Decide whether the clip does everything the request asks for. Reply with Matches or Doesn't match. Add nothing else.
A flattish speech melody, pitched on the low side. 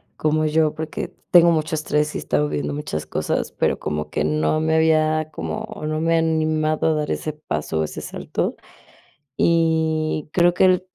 Doesn't match